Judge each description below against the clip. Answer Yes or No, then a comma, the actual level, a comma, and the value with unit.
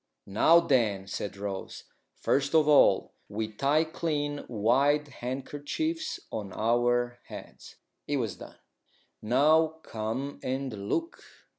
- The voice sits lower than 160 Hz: Yes, low, 135 Hz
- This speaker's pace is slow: Yes, slow, 115 wpm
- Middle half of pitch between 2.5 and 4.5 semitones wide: No, average, 5.1 semitones